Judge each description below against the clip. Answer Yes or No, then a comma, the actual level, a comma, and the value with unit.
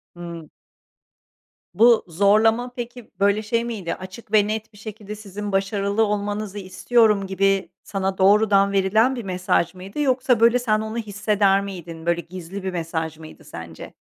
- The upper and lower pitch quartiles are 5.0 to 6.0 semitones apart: No, average, 2.7 semitones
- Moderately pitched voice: No, high, 200 Hz